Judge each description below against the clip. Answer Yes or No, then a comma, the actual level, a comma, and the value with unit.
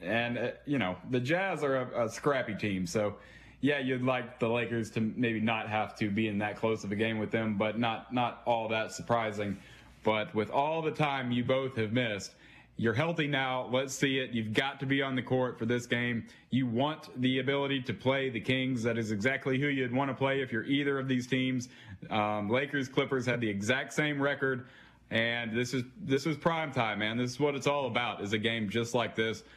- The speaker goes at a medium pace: No, fast, 225 wpm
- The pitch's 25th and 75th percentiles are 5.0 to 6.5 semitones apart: No, average, 3.4 semitones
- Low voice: Yes, low, 125 Hz